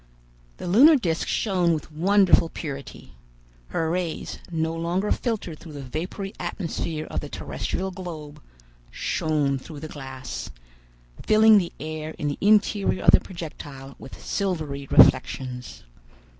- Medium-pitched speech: Yes, medium, 160 Hz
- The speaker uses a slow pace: Yes, slow, 130 wpm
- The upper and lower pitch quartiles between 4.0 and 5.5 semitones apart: Yes, average, 4.3 semitones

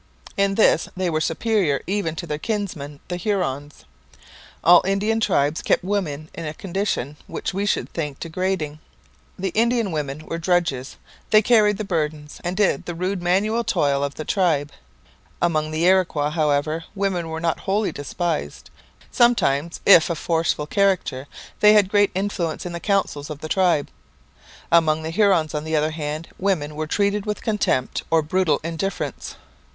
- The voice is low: No, medium, 170 Hz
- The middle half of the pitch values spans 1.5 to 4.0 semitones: No, average, 4.4 semitones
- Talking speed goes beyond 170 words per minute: No, average, 165 wpm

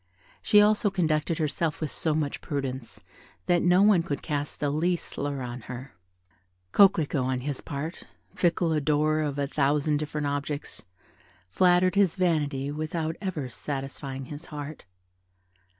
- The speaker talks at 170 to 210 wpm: No, average, 140 wpm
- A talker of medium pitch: Yes, medium, 150 Hz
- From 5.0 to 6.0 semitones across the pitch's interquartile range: No, average, 3.0 semitones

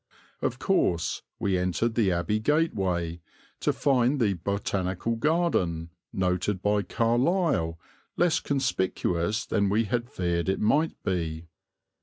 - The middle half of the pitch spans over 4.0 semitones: Yes, average, 5.2 semitones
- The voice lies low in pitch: Yes, low, 100 Hz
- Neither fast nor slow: No, slow, 120 wpm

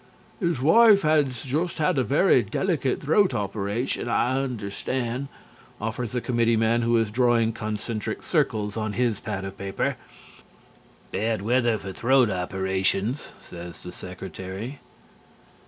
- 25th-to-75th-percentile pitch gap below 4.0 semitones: No, average, 4.4 semitones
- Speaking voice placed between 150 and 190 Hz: No, low, 115 Hz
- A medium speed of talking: No, slow, 125 wpm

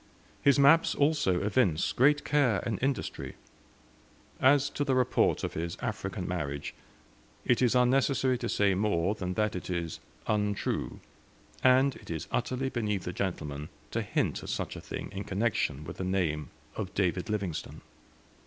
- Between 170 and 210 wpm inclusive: No, average, 155 wpm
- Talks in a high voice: No, low, 105 Hz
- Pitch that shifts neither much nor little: No, wide, 6.1 semitones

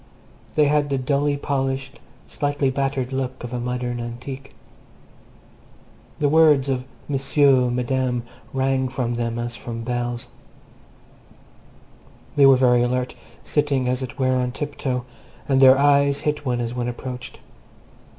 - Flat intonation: Yes, narrow, 2.1 semitones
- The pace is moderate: No, slow, 130 wpm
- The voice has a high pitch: No, low, 130 Hz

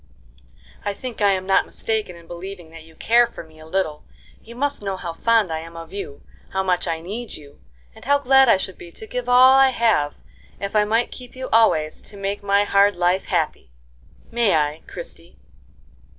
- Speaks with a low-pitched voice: No, high, 200 Hz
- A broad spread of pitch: Yes, wide, 5.7 semitones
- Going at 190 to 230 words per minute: Yes, fast, 205 wpm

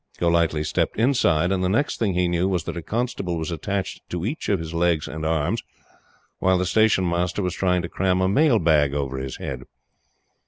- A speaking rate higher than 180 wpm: Yes, average, 200 wpm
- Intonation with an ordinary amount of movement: Yes, average, 3.0 semitones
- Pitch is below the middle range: Yes, very low, 90 Hz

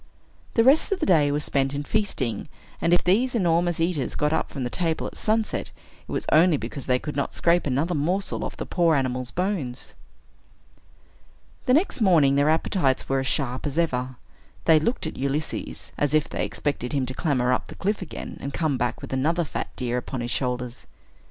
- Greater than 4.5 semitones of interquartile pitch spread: Yes, average, 5.0 semitones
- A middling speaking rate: Yes, average, 195 wpm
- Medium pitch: Yes, medium, 150 Hz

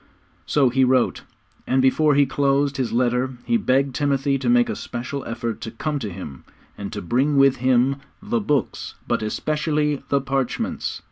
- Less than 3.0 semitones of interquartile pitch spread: Yes, narrow, 2.5 semitones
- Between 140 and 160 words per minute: No, average, 175 wpm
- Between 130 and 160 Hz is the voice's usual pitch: Yes, low, 135 Hz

